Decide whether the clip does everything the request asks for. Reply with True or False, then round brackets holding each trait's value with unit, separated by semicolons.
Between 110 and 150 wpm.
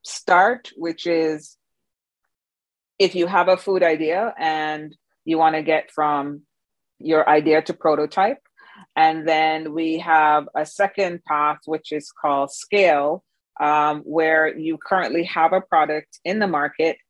True (140 wpm)